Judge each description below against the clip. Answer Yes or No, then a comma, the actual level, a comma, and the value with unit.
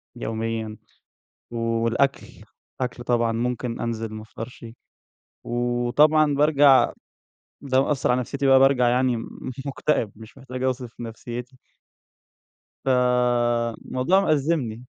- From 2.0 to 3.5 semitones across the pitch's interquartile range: Yes, narrow, 2.4 semitones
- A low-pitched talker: Yes, low, 125 Hz